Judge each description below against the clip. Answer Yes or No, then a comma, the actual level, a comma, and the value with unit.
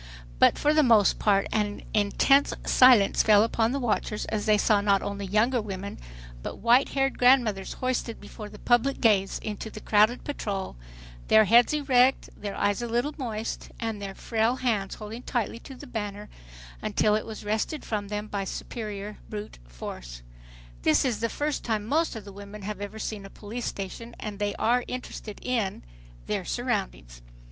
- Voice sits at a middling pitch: No, high, 215 Hz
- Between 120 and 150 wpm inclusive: No, average, 170 wpm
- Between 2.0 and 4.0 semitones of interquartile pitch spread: Yes, average, 3.0 semitones